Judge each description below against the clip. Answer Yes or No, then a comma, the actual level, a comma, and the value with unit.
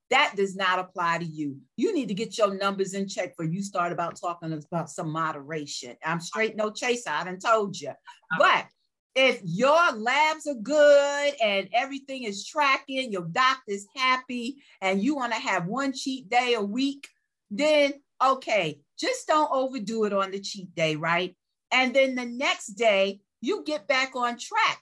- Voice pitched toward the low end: No, high, 225 Hz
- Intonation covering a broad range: Yes, wide, 6.7 semitones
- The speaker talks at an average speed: Yes, average, 175 wpm